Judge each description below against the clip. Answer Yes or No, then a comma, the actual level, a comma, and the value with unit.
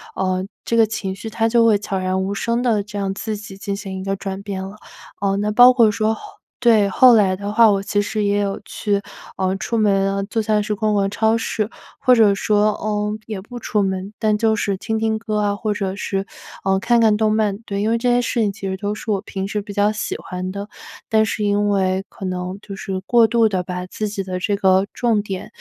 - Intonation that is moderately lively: No, narrow, 2.0 semitones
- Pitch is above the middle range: Yes, high, 205 Hz